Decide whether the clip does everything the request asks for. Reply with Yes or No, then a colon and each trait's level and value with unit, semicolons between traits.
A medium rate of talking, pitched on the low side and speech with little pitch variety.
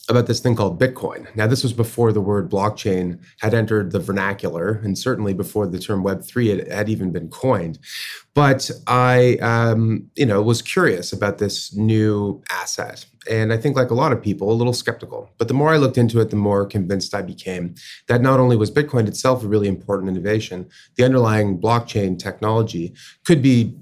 No: average, 195 wpm; low, 110 Hz; average, 3.5 semitones